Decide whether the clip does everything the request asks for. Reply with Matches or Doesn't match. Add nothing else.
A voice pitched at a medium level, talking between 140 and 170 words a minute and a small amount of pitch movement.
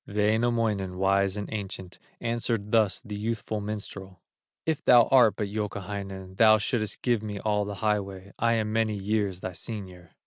Doesn't match